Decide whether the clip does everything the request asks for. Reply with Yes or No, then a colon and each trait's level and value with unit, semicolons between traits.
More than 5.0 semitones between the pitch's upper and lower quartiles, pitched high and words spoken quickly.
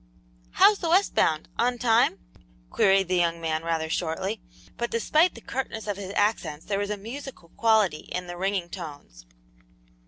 No: wide, 5.5 semitones; high, 195 Hz; average, 165 wpm